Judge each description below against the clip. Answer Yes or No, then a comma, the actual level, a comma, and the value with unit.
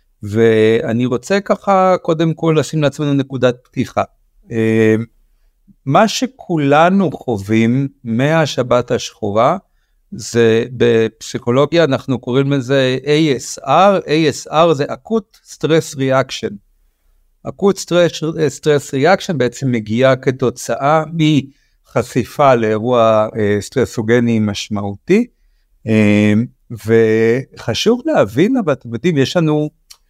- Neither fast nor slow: No, slow, 85 wpm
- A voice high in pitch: No, low, 130 Hz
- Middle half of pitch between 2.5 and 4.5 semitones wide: No, wide, 5.6 semitones